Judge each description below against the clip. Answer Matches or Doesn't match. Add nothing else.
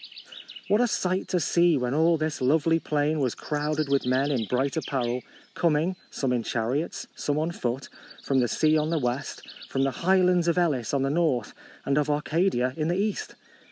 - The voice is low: Doesn't match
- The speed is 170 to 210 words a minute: Matches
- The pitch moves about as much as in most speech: Matches